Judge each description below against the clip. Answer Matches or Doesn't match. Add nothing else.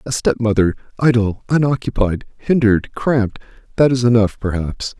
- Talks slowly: Matches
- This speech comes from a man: Matches